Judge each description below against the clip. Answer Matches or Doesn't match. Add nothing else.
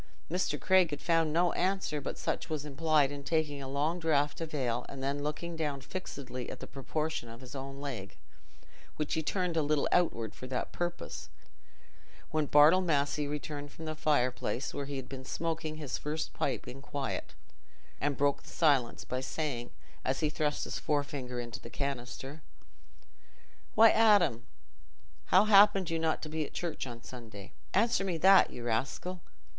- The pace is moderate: Matches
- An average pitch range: Matches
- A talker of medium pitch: Matches